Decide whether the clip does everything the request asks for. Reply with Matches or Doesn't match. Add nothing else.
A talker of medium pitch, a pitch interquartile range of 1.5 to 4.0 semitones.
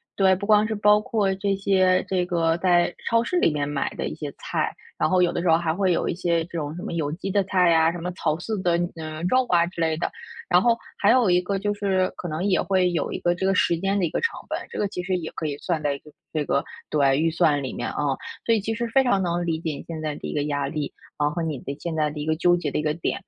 Matches